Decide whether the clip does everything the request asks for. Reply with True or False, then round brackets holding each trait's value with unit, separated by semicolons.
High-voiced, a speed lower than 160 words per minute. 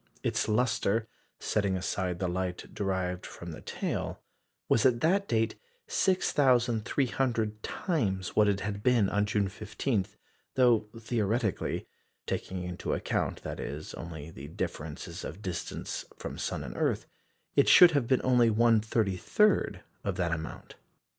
False (105 Hz; 135 wpm)